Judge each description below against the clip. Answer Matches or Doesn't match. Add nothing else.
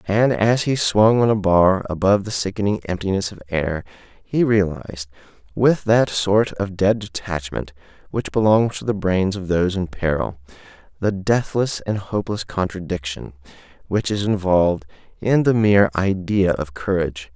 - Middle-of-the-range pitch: Doesn't match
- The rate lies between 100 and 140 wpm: Doesn't match